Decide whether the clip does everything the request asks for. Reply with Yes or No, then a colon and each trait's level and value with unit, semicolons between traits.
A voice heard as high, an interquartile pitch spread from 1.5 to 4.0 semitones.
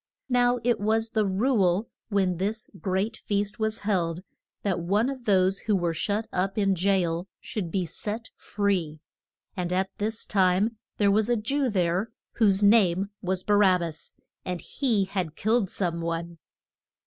Yes: high, 200 Hz; average, 3.2 semitones